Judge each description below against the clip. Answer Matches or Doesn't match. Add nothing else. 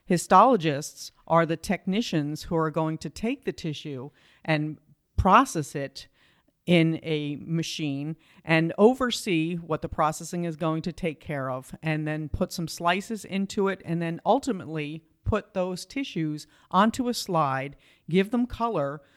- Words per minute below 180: Matches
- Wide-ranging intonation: Doesn't match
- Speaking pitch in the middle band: Matches